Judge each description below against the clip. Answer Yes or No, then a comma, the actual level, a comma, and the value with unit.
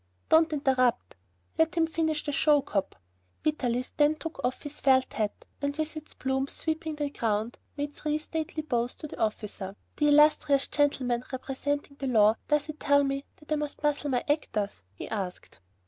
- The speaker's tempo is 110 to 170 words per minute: No, average, 180 wpm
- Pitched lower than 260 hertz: No, very high, 285 Hz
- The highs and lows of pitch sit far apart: No, average, 3.4 semitones